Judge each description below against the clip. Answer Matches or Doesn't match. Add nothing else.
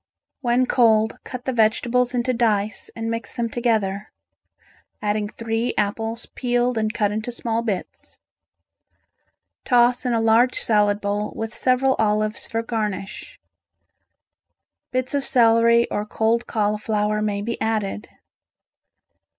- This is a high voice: Matches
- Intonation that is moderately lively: Doesn't match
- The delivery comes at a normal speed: Doesn't match